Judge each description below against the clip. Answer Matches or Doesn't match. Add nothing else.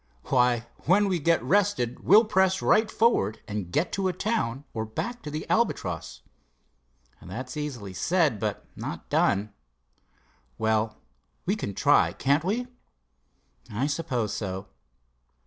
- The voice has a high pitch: Doesn't match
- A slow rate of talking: Matches